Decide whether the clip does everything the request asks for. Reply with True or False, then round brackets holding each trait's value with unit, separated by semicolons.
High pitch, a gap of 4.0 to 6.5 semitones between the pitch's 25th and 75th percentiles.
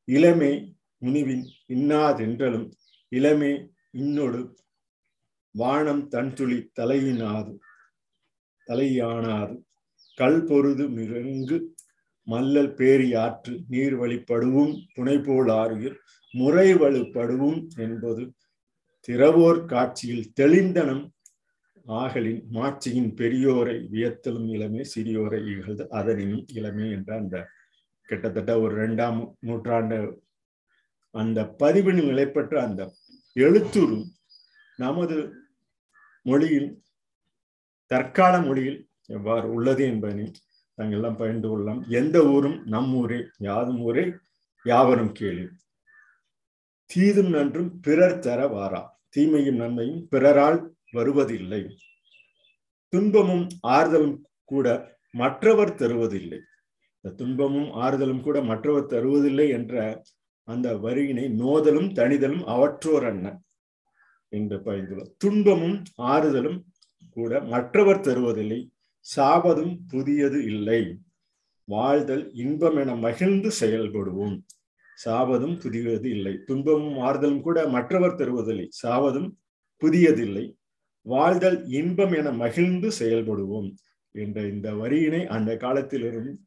False (130 Hz; 4.9 semitones)